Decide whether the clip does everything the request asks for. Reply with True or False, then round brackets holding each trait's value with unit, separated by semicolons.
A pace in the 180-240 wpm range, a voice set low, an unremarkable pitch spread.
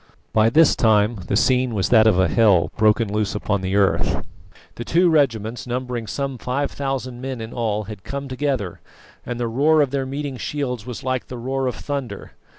True (190 wpm; 125 Hz; 3.8 semitones)